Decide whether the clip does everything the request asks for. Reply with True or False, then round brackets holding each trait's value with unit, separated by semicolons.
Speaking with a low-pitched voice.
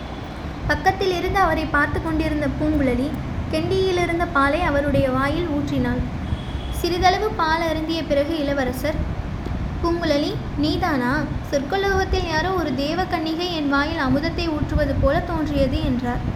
False (320 Hz)